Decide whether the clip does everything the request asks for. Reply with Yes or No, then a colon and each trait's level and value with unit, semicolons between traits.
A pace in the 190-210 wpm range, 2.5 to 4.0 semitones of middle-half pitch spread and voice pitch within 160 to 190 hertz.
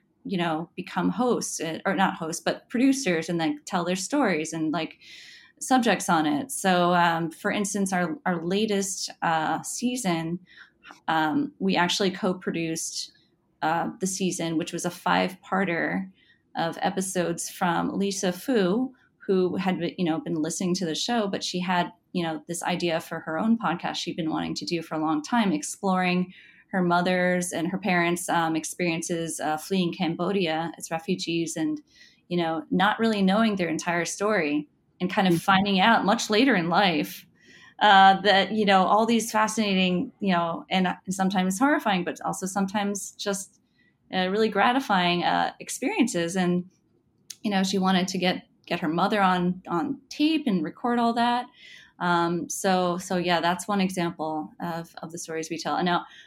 No: average, 170 wpm; average, 3.2 semitones; medium, 185 Hz